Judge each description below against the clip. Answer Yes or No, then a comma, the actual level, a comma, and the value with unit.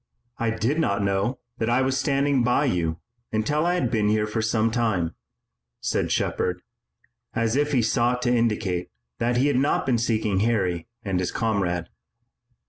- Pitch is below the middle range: Yes, low, 115 Hz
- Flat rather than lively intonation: No, average, 4.0 semitones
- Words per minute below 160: No, average, 165 wpm